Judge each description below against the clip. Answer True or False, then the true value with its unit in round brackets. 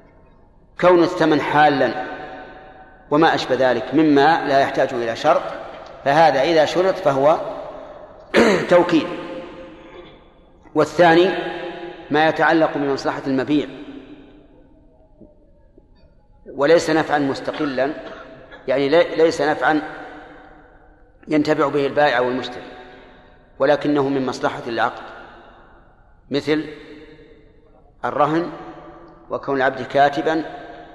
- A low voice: False (150 Hz)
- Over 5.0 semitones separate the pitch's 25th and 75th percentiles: False (3.2 semitones)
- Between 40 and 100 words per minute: True (80 wpm)